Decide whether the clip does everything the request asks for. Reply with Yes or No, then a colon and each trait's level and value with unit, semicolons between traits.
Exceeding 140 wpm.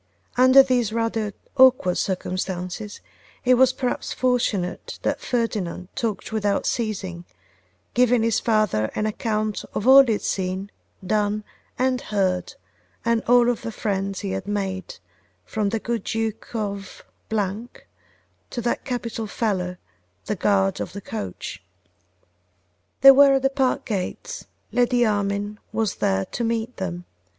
No: slow, 135 wpm